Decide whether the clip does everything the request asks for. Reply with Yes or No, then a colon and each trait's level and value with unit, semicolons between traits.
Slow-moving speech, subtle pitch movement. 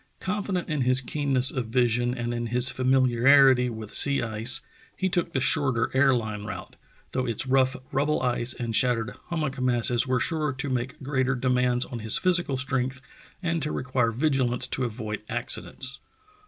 No: average, 170 wpm; narrow, 2.2 semitones